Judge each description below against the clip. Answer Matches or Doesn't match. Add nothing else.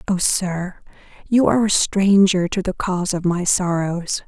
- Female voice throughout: Matches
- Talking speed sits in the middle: Matches